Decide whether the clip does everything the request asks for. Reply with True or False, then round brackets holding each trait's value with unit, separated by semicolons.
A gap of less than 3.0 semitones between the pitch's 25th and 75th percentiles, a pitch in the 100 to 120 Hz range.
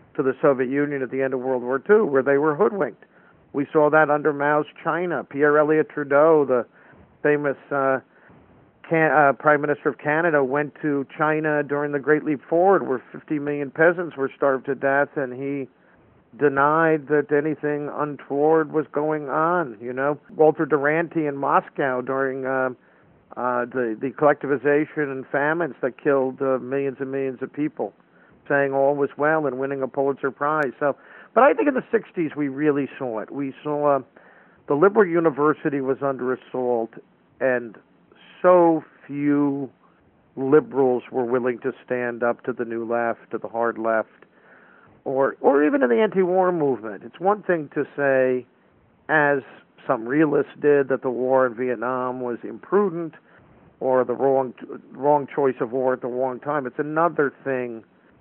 False (2.5 semitones; 140 Hz)